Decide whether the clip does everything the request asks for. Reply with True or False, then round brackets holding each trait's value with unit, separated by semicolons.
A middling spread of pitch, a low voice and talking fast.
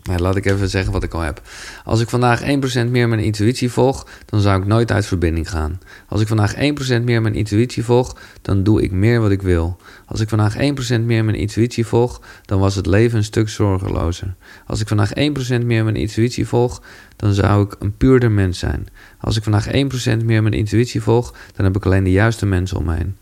True (3.2 semitones; 105 Hz; 225 wpm)